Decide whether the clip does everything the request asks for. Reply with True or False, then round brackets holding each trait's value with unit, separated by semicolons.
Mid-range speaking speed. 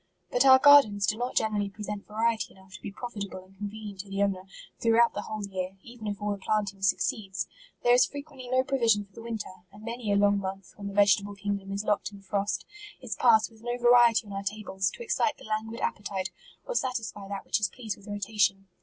False (245 wpm)